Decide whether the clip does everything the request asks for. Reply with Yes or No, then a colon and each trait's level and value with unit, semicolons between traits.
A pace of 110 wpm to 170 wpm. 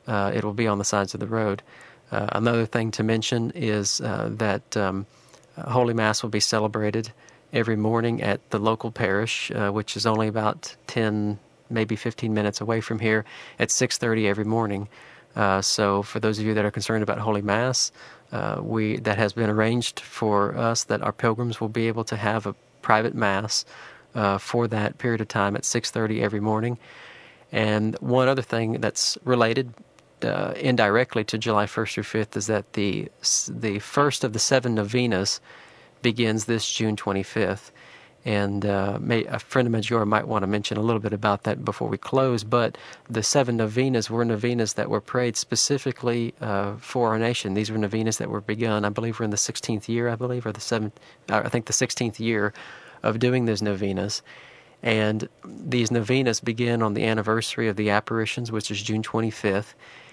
No: average, 190 wpm